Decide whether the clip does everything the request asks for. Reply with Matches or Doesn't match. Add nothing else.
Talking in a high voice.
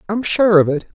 Matches